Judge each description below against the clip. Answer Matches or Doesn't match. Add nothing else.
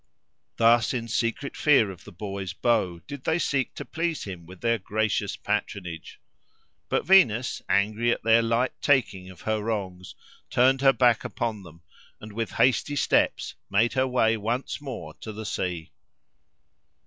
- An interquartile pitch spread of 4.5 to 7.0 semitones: Doesn't match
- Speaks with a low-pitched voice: Matches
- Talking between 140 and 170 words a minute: Matches